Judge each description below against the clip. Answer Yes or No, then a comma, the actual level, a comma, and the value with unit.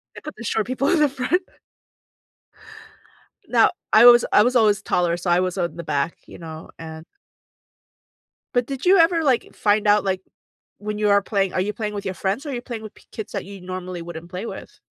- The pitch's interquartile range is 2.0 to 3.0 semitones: No, average, 5.1 semitones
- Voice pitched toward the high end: Yes, high, 205 Hz